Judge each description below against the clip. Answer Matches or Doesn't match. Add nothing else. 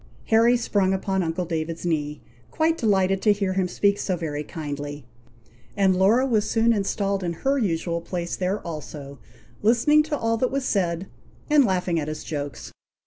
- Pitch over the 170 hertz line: Matches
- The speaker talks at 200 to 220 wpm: Doesn't match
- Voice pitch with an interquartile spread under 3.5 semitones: Doesn't match